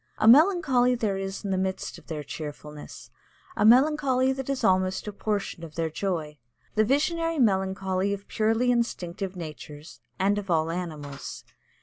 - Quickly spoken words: No, average, 155 wpm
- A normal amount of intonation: No, wide, 6.4 semitones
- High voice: Yes, high, 195 Hz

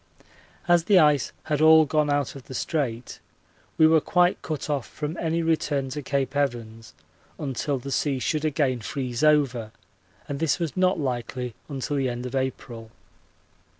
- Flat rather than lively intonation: No, average, 3.5 semitones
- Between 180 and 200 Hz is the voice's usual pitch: No, medium, 140 Hz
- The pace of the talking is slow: No, average, 165 wpm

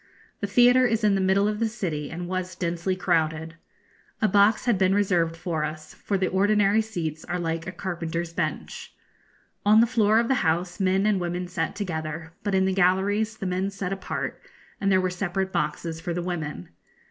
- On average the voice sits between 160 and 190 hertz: Yes, medium, 185 Hz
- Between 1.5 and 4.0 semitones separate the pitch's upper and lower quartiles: Yes, average, 3.2 semitones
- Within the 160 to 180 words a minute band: No, average, 195 wpm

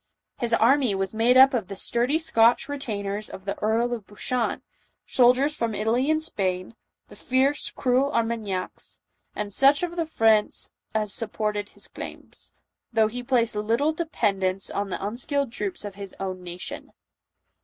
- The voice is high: Yes, high, 230 Hz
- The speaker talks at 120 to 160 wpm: Yes, average, 155 wpm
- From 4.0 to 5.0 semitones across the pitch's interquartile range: Yes, average, 4.4 semitones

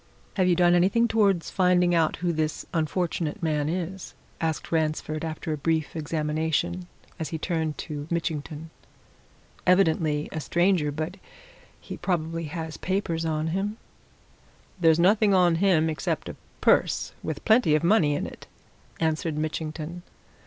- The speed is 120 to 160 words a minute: Yes, average, 140 wpm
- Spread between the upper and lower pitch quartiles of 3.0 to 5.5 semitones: No, narrow, 2.4 semitones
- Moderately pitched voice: Yes, medium, 165 Hz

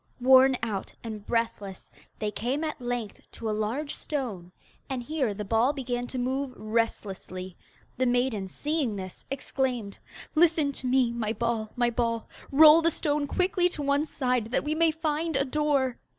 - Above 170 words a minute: No, average, 165 wpm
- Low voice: No, very high, 250 Hz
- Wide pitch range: No, average, 4.5 semitones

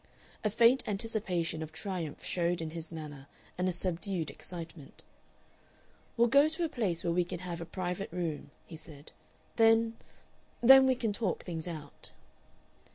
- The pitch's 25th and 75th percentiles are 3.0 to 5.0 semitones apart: No, wide, 5.4 semitones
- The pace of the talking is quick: No, average, 160 wpm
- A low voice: No, medium, 180 Hz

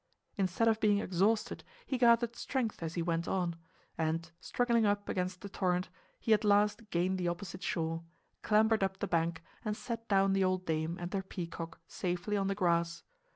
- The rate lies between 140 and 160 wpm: No, average, 185 wpm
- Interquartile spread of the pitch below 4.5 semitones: Yes, average, 3.6 semitones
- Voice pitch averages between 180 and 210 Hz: Yes, high, 190 Hz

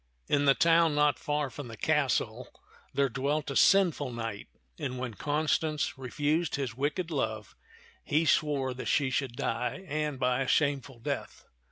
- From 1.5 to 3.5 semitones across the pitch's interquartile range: Yes, average, 2.9 semitones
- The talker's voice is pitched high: No, medium, 140 Hz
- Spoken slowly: No, average, 160 wpm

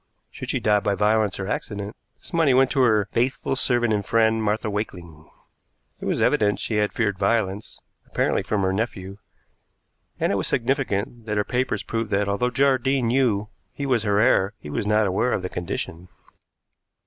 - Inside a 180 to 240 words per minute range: Yes, average, 185 wpm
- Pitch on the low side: Yes, low, 105 Hz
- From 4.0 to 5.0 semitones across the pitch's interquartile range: No, average, 3.3 semitones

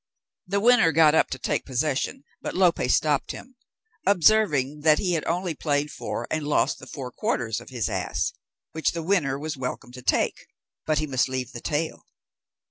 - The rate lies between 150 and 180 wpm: No, average, 190 wpm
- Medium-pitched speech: Yes, medium, 150 Hz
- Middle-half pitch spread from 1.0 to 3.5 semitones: No, average, 4.2 semitones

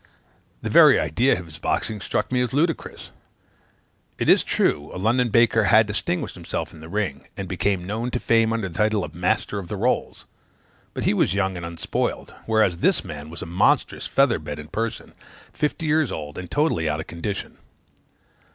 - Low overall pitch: Yes, low, 100 Hz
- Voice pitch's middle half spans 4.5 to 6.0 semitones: Yes, average, 5.2 semitones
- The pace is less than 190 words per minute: No, average, 195 wpm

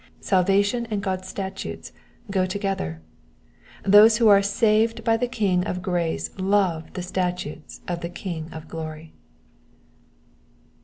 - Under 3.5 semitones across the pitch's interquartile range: Yes, average, 2.9 semitones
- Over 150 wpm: No, slow, 135 wpm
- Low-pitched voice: No, high, 190 Hz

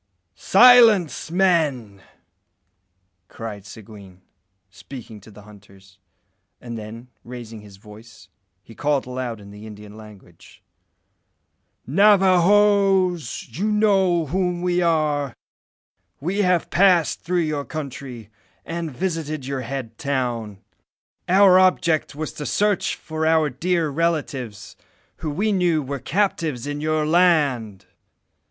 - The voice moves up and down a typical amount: No, wide, 7.7 semitones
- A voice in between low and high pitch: Yes, medium, 150 Hz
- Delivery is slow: Yes, slow, 115 wpm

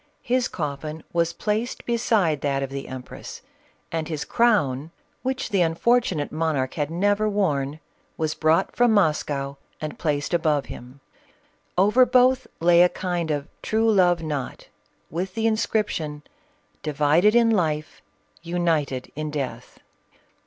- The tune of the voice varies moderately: No, wide, 6.0 semitones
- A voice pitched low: No, medium, 165 Hz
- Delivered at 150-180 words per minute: No, average, 140 wpm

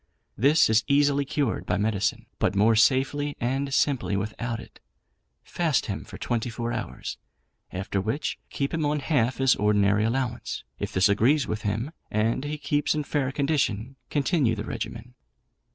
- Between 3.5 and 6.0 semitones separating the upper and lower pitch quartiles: Yes, average, 4.8 semitones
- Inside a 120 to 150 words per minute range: No, average, 160 wpm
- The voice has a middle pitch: No, low, 125 Hz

